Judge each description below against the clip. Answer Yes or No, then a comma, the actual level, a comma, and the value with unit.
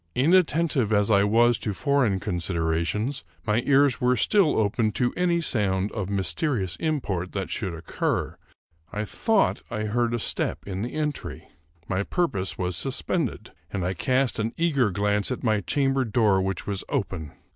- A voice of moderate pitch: No, low, 110 Hz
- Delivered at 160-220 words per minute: Yes, average, 165 wpm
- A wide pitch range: Yes, wide, 5.8 semitones